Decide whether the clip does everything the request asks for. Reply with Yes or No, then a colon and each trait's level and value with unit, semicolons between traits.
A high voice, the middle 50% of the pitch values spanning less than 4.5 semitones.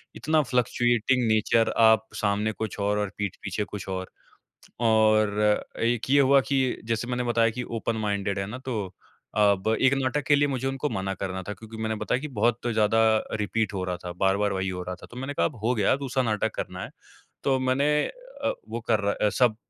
No: low, 110 Hz; average, 3.7 semitones